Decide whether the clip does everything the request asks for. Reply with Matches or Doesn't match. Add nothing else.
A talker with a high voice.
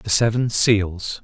Doesn't match